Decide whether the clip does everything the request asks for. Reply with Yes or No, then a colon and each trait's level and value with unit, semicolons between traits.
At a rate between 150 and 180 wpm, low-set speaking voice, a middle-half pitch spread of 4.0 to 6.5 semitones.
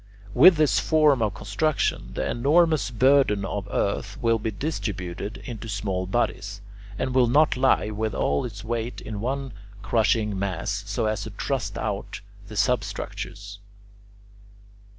No: average, 140 wpm; low, 110 Hz; average, 4.5 semitones